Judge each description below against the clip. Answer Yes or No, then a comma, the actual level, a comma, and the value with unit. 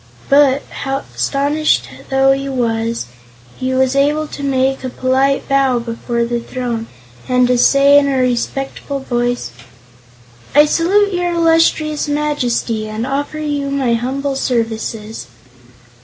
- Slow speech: Yes, slow, 125 wpm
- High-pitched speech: Yes, very high, 270 Hz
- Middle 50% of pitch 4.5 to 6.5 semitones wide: No, average, 2.9 semitones